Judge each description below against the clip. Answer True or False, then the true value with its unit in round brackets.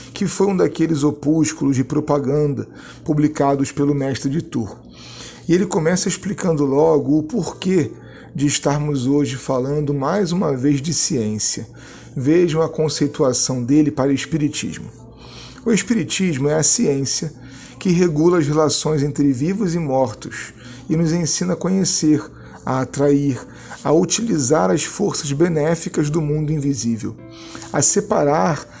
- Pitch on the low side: False (150 Hz)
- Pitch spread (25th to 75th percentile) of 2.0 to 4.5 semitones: True (3.2 semitones)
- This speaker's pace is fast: False (135 wpm)